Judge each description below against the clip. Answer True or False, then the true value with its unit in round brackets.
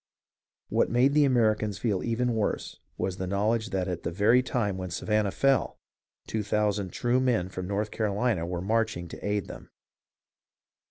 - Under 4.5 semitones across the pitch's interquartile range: True (3.6 semitones)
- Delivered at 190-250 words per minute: False (170 wpm)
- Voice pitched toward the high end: False (105 Hz)